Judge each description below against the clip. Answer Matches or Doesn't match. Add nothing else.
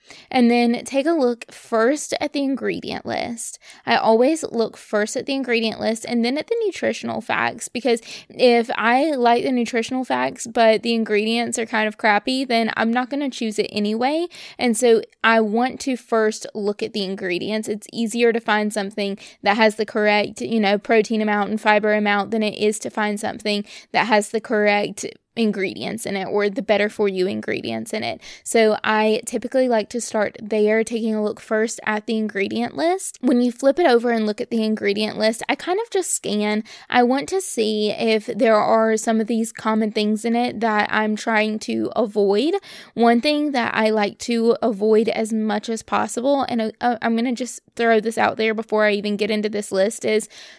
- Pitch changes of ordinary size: Doesn't match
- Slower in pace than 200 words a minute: Doesn't match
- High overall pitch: Matches